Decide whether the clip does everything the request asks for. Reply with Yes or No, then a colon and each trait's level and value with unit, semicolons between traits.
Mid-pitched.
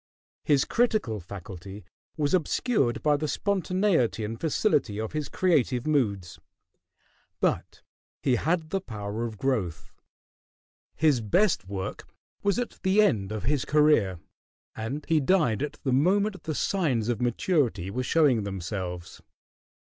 No: low, 130 Hz